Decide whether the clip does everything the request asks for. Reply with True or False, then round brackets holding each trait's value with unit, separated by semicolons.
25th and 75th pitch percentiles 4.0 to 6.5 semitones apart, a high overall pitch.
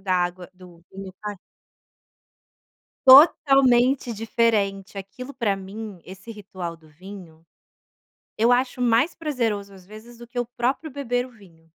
True (4.5 semitones; 215 Hz)